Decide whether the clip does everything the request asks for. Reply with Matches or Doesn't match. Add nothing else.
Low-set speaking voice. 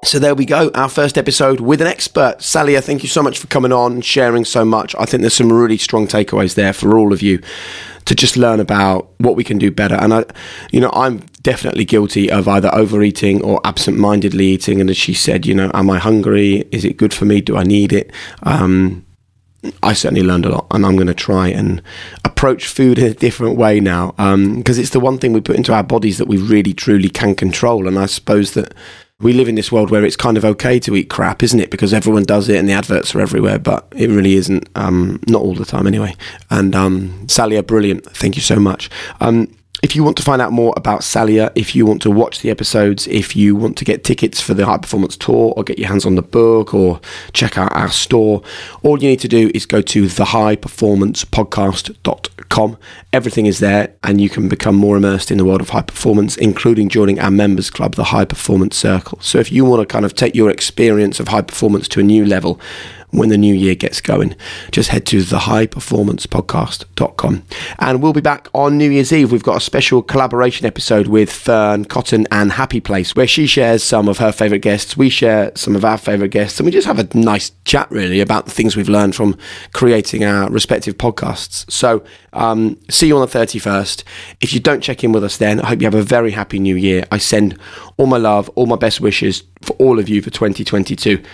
Matches